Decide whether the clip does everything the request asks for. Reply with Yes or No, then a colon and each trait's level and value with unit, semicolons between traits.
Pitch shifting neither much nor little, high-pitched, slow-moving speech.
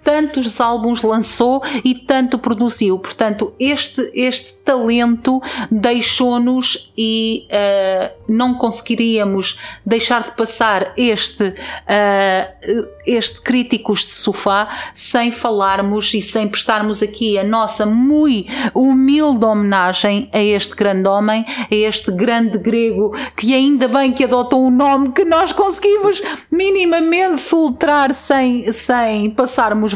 Yes: average, 3.6 semitones; high, 235 Hz; slow, 115 wpm